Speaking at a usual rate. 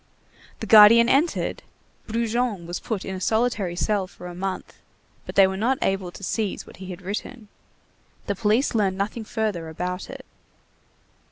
Yes: average, 165 wpm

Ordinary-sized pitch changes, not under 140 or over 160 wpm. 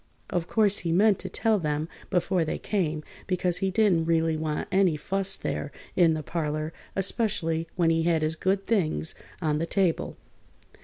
No: average, 3.3 semitones; average, 170 wpm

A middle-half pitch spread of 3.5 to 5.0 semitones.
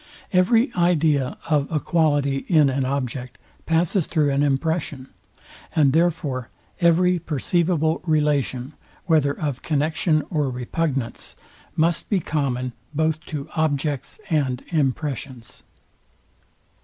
No: average, 3.1 semitones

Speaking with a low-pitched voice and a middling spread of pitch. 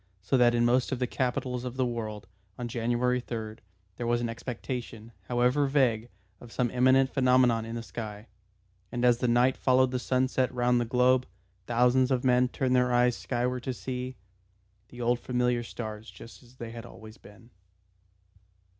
No: low, 125 Hz; narrow, 1.3 semitones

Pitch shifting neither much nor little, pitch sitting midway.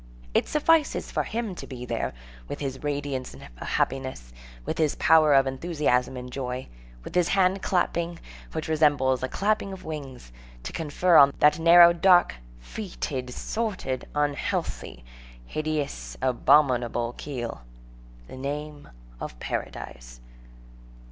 Yes: average, 4.8 semitones; medium, 145 Hz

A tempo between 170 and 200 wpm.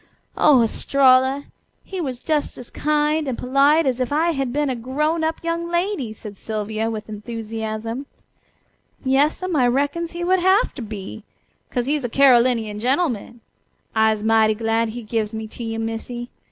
No: average, 160 wpm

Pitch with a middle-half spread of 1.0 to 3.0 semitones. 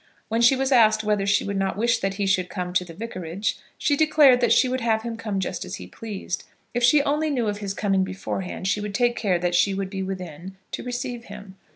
No: average, 3.9 semitones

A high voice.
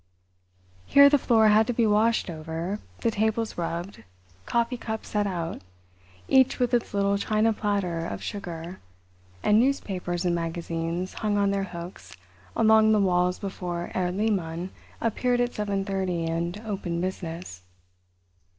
Yes: high, 195 Hz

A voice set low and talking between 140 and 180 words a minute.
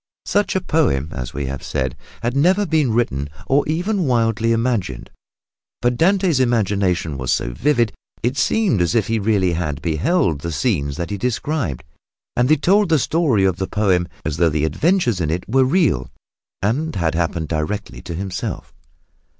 Yes: low, 105 Hz; average, 175 wpm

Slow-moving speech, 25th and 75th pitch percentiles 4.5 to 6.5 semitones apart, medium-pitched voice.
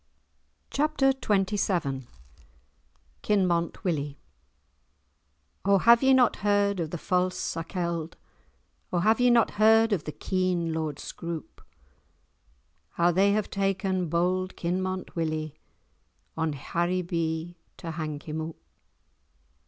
No: slow, 110 wpm; average, 3.6 semitones; medium, 180 Hz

